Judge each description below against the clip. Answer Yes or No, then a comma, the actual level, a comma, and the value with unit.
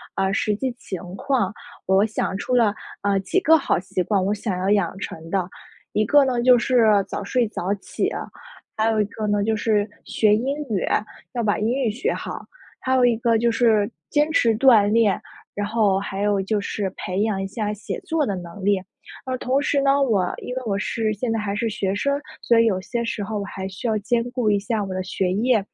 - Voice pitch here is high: Yes, high, 215 Hz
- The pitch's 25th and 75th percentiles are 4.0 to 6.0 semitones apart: No, average, 3.3 semitones